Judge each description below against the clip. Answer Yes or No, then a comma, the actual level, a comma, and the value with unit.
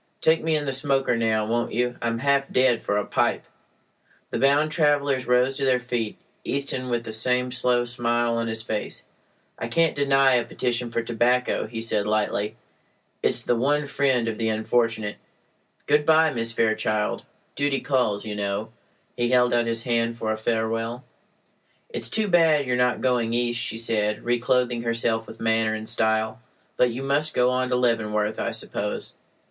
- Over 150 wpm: Yes, average, 180 wpm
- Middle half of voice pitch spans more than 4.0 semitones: No, average, 2.7 semitones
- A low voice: Yes, low, 120 Hz